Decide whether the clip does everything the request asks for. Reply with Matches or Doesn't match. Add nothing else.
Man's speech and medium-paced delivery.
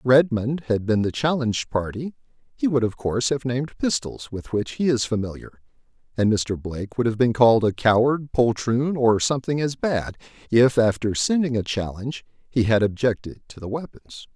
Matches